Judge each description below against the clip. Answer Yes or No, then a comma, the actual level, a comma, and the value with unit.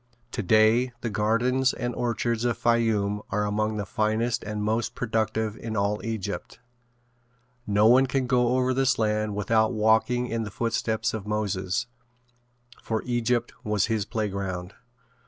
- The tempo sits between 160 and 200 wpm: No, average, 140 wpm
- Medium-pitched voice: No, low, 110 Hz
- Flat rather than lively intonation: Yes, narrow, 2.2 semitones